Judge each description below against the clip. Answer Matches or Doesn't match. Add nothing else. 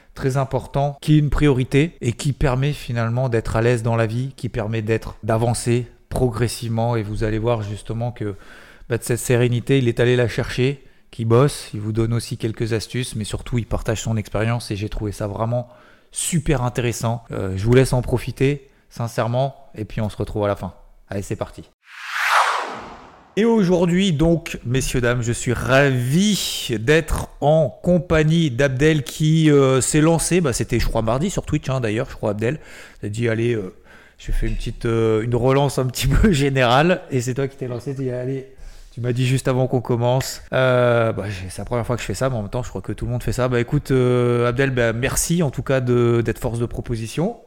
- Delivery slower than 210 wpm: Doesn't match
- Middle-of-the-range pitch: Doesn't match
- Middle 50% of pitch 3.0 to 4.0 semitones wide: Matches